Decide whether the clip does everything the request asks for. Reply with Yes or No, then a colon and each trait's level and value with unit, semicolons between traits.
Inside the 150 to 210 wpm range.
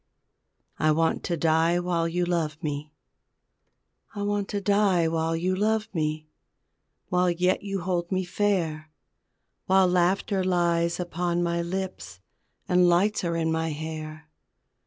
No: slow, 135 wpm